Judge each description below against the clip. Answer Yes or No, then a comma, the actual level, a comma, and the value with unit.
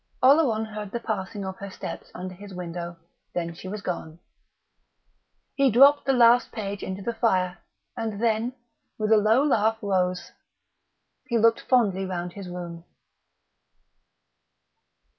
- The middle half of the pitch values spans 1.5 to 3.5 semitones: No, average, 3.9 semitones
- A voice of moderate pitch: No, high, 205 Hz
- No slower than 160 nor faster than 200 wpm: No, average, 140 wpm